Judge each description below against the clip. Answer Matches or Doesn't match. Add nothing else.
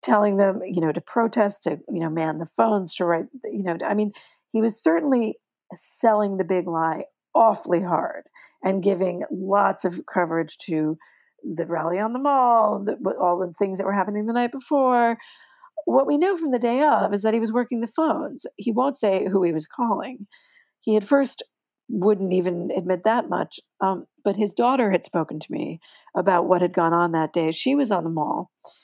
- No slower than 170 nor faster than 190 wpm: Doesn't match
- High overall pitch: Matches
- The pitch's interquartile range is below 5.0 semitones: Doesn't match